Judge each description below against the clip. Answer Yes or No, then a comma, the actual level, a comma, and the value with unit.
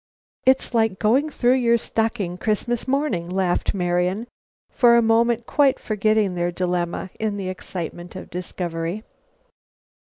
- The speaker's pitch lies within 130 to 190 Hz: No, high, 210 Hz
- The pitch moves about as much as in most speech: Yes, average, 4.8 semitones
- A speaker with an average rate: No, slow, 130 wpm